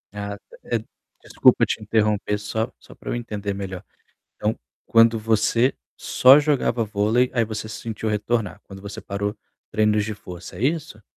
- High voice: No, low, 110 Hz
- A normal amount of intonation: No, narrow, 1.9 semitones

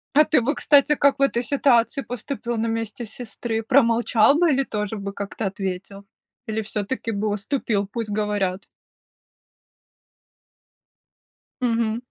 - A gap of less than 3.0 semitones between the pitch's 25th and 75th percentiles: No, average, 3.4 semitones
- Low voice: No, high, 225 Hz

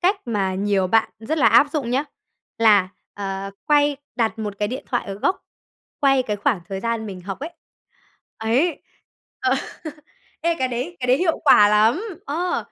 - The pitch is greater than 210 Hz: Yes, high, 230 Hz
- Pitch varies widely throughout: Yes, wide, 5.8 semitones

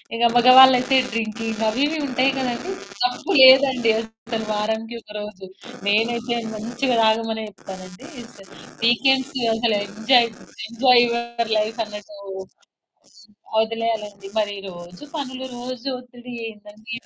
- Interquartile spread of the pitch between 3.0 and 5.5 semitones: No, narrow, 2.5 semitones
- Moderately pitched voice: No, high, 230 Hz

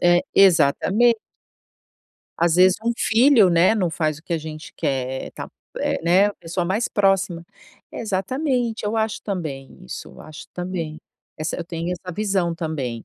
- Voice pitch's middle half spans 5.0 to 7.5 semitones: No, average, 4.2 semitones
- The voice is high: No, medium, 180 Hz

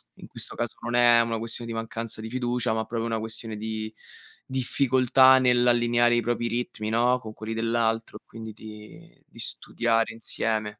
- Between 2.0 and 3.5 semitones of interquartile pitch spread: No, narrow, 1.4 semitones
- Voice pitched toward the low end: Yes, low, 115 Hz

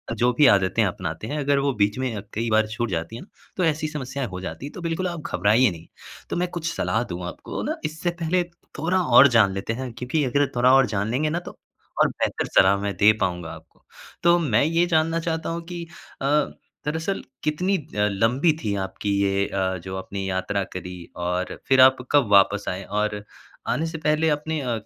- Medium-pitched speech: No, low, 125 Hz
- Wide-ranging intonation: Yes, wide, 7.9 semitones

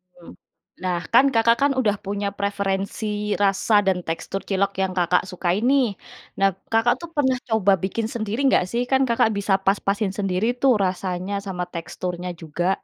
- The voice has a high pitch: Yes, high, 200 Hz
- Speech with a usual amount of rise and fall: Yes, average, 3.3 semitones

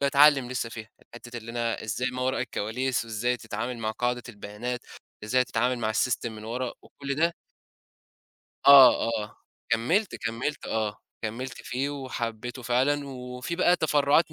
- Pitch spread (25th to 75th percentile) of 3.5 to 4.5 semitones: No, average, 2.8 semitones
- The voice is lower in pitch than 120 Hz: No, low, 125 Hz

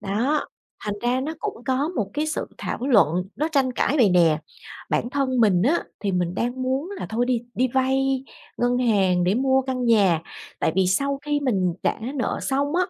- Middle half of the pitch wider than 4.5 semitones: Yes, average, 5.3 semitones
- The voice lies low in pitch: No, very high, 250 Hz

